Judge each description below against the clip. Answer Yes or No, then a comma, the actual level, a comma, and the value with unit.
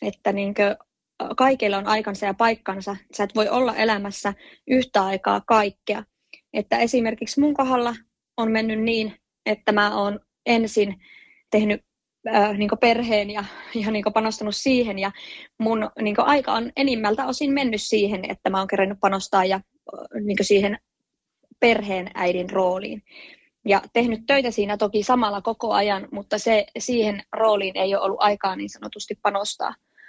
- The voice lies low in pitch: No, high, 210 Hz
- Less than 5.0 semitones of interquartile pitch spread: Yes, narrow, 2.4 semitones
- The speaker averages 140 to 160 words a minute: Yes, average, 150 wpm